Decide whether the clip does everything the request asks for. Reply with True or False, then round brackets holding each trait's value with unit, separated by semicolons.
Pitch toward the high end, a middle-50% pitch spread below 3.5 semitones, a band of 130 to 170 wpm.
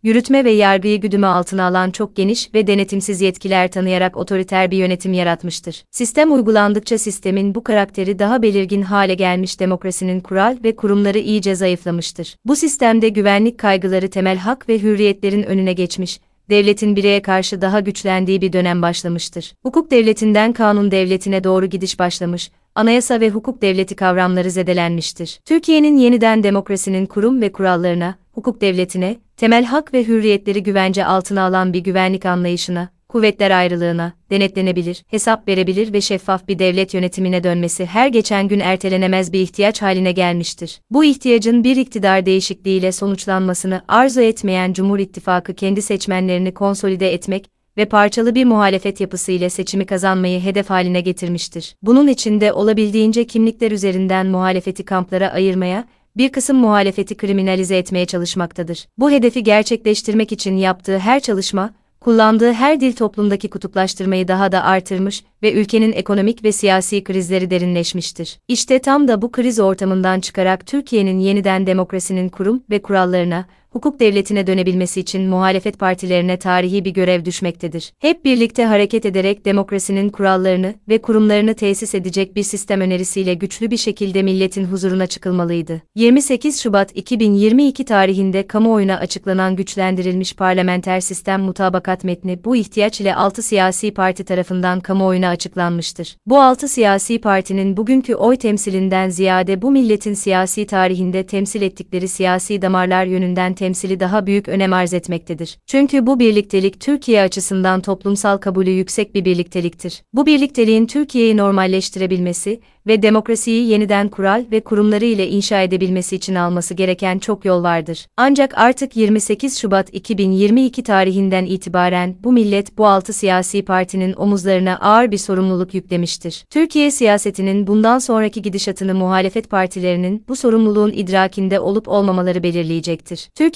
True (195 Hz; 2.5 semitones; 135 wpm)